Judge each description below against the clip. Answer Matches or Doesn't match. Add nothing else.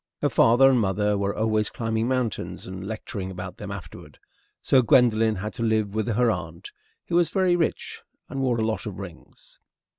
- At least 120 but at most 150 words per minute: Doesn't match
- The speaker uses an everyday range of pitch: Matches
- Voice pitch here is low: Matches